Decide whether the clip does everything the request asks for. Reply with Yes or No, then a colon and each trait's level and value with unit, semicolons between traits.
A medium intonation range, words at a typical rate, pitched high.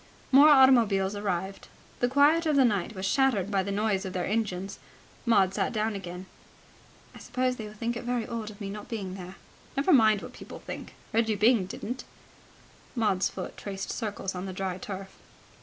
Yes: average, 3.7 semitones; average, 190 wpm; high, 210 Hz